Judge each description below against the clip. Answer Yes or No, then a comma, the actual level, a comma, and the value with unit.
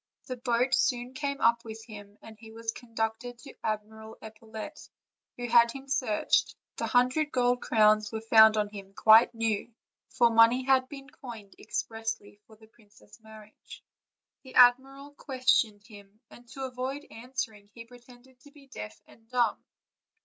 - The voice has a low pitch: No, high, 230 Hz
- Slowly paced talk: No, average, 160 wpm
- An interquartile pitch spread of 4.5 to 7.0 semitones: No, narrow, 2.5 semitones